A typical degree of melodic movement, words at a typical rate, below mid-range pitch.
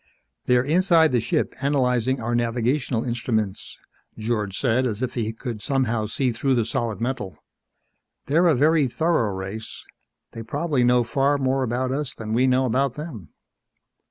Yes: average, 3.3 semitones; average, 155 wpm; low, 125 Hz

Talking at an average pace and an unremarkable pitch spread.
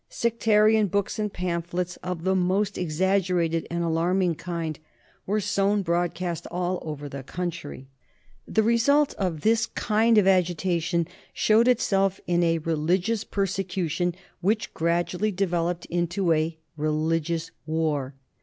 No: slow, 125 wpm; average, 3.2 semitones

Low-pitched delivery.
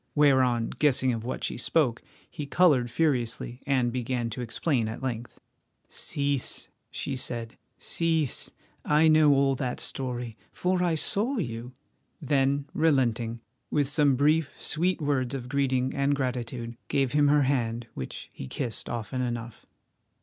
Yes: low, 130 Hz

